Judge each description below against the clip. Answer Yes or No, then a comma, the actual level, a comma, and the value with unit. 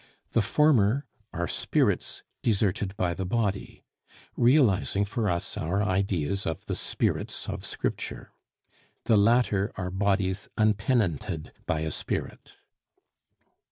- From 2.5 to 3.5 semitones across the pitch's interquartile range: Yes, average, 3.0 semitones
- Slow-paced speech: Yes, slow, 115 wpm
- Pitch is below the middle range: Yes, low, 100 Hz